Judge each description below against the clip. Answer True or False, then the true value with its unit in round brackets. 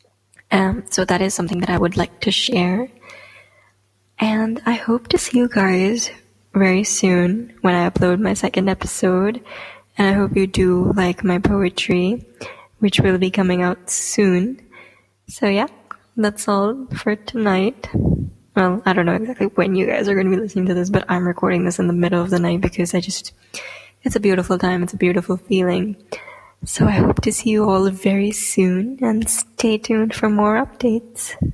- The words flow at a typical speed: True (185 wpm)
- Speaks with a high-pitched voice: True (195 Hz)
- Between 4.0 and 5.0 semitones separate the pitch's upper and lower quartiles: False (3.2 semitones)